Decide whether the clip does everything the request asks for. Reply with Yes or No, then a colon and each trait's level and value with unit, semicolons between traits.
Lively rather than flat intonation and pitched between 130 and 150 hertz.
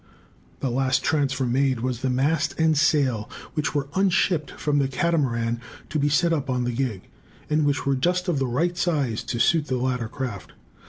No: average, 3.5 semitones; low, 135 Hz